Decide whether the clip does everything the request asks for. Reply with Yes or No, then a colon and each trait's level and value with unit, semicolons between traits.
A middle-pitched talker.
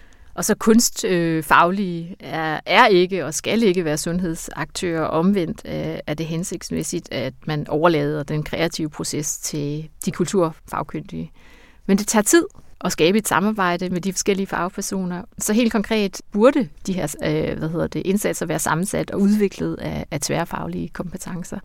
Yes: medium, 175 Hz